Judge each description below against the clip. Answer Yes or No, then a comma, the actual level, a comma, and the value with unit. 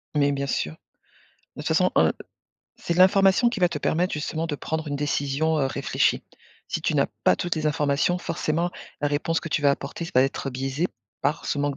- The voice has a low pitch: No, medium, 150 Hz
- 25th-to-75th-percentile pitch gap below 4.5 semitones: Yes, average, 3.1 semitones